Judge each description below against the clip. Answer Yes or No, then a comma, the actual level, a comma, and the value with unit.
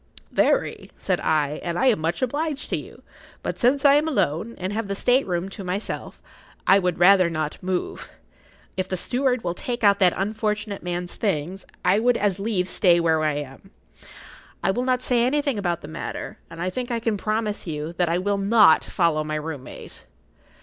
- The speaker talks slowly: No, average, 200 wpm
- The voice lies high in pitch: Yes, high, 195 Hz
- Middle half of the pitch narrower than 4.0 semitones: No, average, 5.2 semitones